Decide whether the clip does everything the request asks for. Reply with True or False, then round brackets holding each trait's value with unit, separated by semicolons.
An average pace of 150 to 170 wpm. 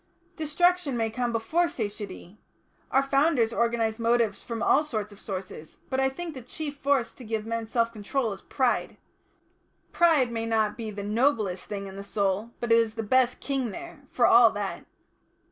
False (180 wpm)